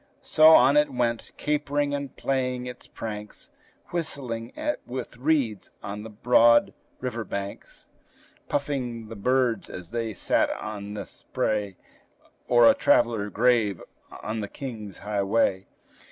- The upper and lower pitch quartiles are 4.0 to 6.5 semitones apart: No, average, 3.6 semitones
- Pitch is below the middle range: Yes, low, 115 Hz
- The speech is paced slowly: Yes, slow, 125 wpm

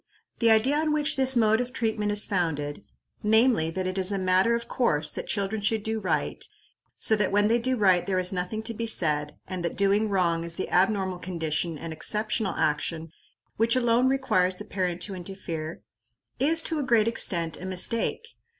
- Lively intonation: No, average, 4.4 semitones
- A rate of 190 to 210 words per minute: Yes, average, 195 wpm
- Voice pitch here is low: No, high, 200 Hz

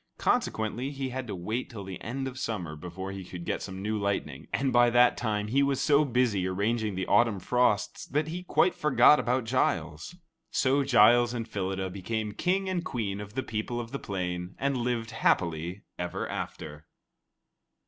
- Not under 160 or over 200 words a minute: Yes, average, 180 wpm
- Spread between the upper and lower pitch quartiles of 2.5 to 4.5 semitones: No, average, 5.1 semitones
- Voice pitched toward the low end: Yes, low, 110 Hz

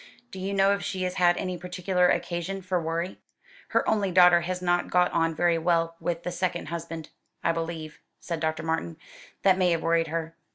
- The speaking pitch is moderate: Yes, medium, 175 Hz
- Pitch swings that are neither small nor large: No, narrow, 1.7 semitones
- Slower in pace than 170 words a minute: No, average, 200 wpm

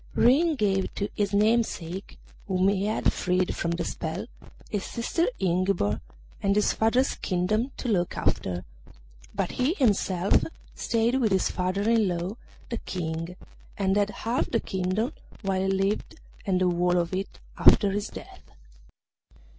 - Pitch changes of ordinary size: Yes, average, 3.4 semitones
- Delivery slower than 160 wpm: Yes, average, 150 wpm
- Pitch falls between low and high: No, high, 195 Hz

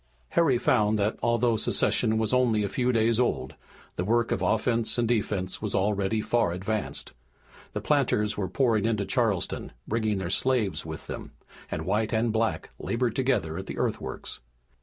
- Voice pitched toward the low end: Yes, low, 110 Hz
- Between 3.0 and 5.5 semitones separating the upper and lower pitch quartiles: No, narrow, 2.5 semitones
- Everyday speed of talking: Yes, average, 165 wpm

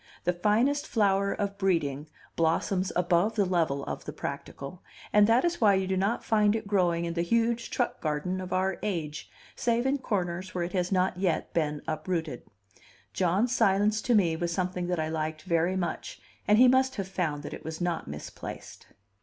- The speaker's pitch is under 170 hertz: No, medium, 185 Hz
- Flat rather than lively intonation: No, average, 3.7 semitones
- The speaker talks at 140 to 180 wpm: No, average, 190 wpm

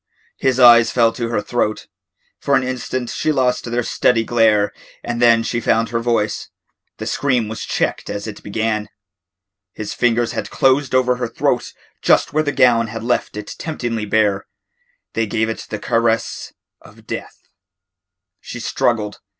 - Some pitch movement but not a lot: No, narrow, 2.1 semitones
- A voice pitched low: Yes, low, 115 Hz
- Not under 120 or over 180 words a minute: Yes, average, 160 wpm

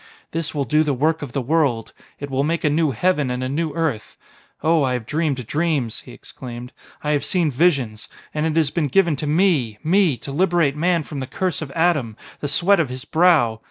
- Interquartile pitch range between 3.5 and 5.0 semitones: Yes, average, 4.1 semitones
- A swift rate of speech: Yes, fast, 220 wpm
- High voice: No, medium, 150 Hz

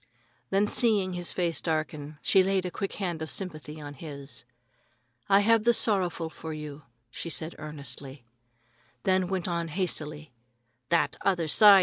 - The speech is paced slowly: No, average, 150 wpm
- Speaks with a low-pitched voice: No, medium, 170 Hz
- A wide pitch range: No, average, 3.9 semitones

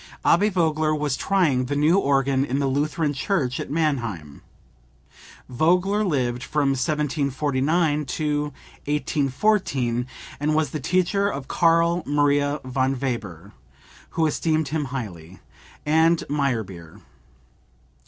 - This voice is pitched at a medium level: Yes, medium, 145 Hz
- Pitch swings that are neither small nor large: Yes, average, 3.5 semitones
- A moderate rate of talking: No, slow, 115 wpm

